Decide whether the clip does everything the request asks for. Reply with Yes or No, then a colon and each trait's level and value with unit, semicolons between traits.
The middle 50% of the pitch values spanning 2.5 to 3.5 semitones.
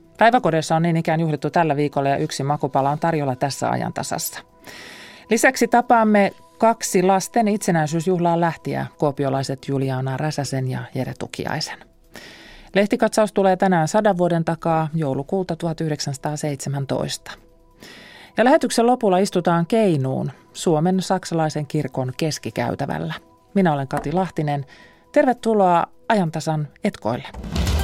No: average, 5.1 semitones